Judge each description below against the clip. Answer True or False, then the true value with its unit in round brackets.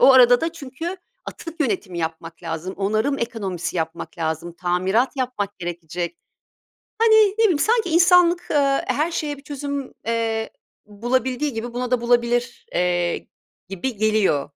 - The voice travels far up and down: True (7.9 semitones)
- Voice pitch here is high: True (235 Hz)